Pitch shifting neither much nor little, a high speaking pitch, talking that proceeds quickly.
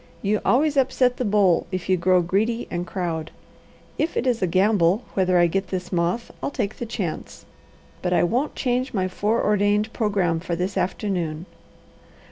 No: average, 4.1 semitones; high, 195 Hz; average, 170 wpm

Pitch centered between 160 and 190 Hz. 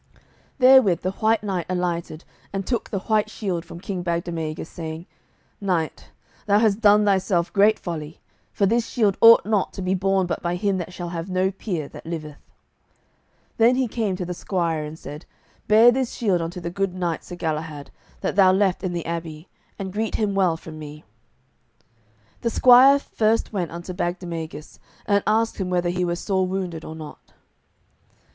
Yes: medium, 185 Hz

